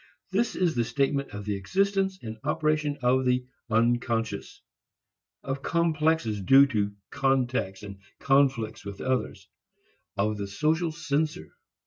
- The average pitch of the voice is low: Yes, low, 130 Hz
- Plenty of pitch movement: Yes, wide, 5.9 semitones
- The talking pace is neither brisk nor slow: No, slow, 125 wpm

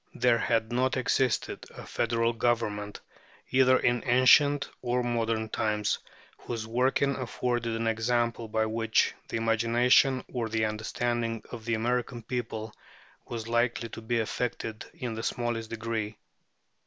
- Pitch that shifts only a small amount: Yes, narrow, 1.5 semitones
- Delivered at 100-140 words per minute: Yes, slow, 135 wpm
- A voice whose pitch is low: Yes, low, 115 Hz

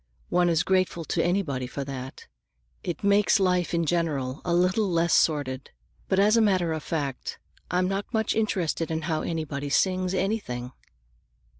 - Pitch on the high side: No, medium, 170 Hz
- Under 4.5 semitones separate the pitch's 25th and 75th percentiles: Yes, average, 4.1 semitones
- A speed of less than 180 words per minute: Yes, average, 160 wpm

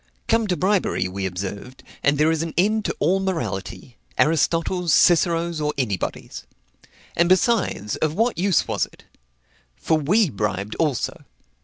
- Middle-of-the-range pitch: Yes, medium, 160 Hz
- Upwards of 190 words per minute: No, average, 145 wpm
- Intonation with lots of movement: Yes, wide, 7.6 semitones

